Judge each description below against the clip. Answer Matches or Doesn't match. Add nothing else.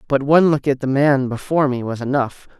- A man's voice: Matches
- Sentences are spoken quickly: Matches